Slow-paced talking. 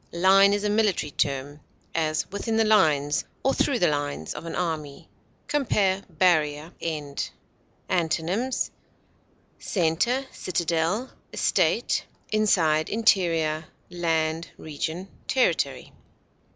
Yes: slow, 100 wpm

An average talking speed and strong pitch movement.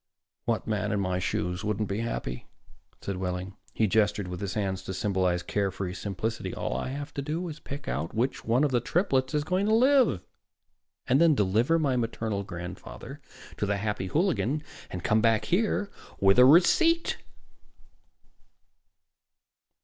Yes: average, 160 wpm; wide, 7.2 semitones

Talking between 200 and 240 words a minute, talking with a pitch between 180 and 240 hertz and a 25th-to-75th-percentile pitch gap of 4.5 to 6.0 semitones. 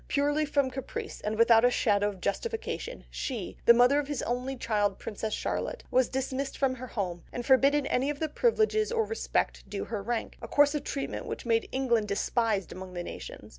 No: fast, 205 wpm; very high, 255 Hz; average, 4.8 semitones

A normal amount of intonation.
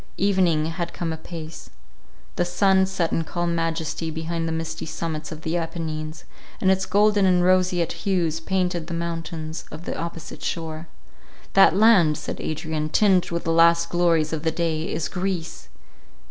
No: narrow, 1.9 semitones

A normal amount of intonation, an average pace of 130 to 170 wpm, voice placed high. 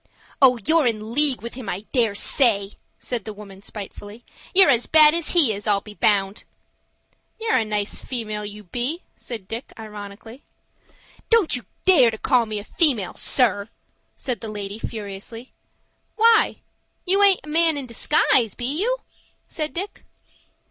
No: wide, 6.3 semitones; average, 160 wpm; high, 235 Hz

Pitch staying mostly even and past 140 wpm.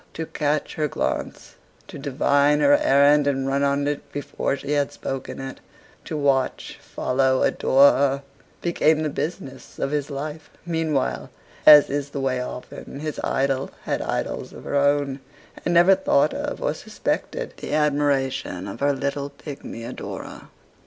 Yes: narrow, 1.6 semitones; average, 155 wpm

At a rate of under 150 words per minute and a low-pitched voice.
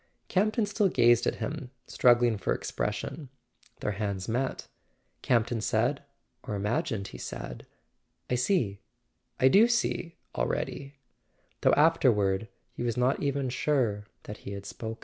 Yes: slow, 135 wpm; low, 120 Hz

